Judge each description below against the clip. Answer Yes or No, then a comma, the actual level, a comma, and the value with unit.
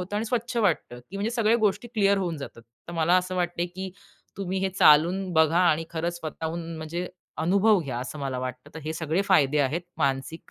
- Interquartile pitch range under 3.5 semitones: No, average, 3.8 semitones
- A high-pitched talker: No, medium, 175 Hz